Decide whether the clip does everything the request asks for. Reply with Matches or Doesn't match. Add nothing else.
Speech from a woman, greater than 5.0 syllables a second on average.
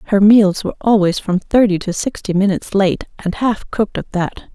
Matches